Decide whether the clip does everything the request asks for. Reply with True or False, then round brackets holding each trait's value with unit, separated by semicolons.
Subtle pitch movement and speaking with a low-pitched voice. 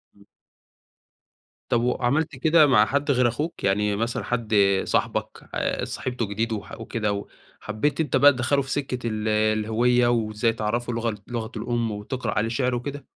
False (3.2 semitones; 120 Hz)